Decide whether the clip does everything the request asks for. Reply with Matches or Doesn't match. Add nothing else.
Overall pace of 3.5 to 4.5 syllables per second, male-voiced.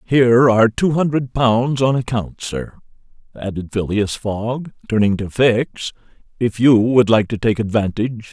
Matches